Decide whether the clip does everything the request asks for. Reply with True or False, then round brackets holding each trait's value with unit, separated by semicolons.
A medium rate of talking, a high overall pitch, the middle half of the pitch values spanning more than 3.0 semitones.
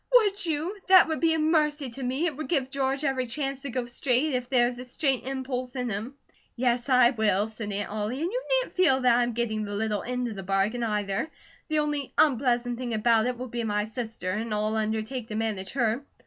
False (230 wpm; 245 Hz; 4.0 semitones)